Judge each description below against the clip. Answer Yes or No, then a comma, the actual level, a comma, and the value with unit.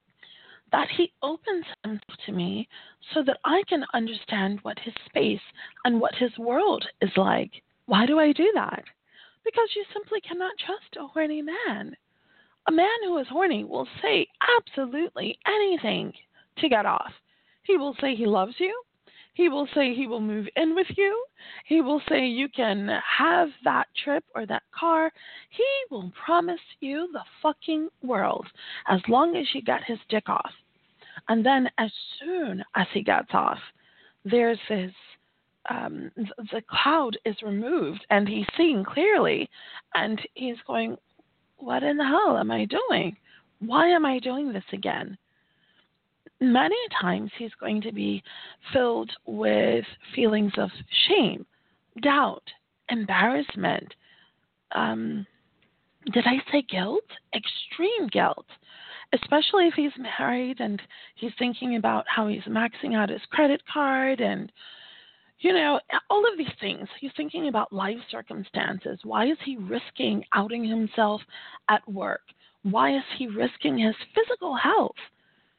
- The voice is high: Yes, very high, 270 Hz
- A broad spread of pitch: Yes, wide, 7.4 semitones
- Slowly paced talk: No, average, 145 wpm